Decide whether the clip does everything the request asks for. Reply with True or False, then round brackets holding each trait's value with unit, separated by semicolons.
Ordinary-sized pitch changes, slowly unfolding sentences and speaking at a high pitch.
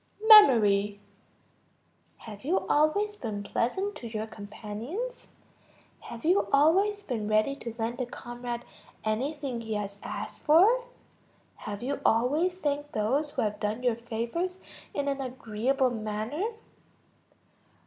False (5.9 semitones; 125 wpm; 245 Hz)